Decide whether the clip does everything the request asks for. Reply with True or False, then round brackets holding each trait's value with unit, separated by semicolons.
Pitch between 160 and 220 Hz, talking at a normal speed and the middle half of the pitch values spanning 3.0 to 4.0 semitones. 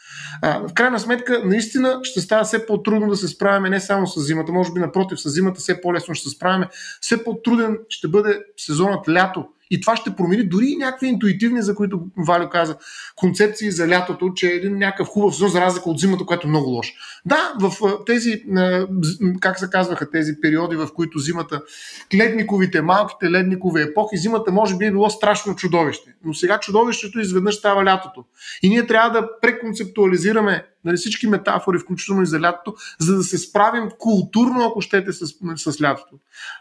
False (190 Hz; 180 wpm; 3.4 semitones)